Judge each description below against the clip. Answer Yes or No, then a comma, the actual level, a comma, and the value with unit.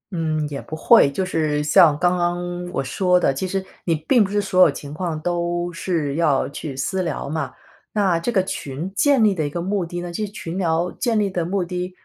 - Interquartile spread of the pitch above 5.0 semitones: No, average, 3.2 semitones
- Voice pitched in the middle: Yes, medium, 175 Hz